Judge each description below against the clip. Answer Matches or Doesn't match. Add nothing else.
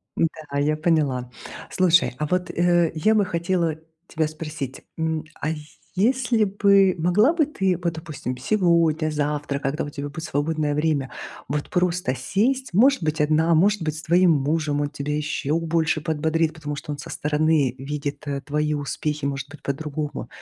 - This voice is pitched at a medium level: Matches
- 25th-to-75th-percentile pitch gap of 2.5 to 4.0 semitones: Matches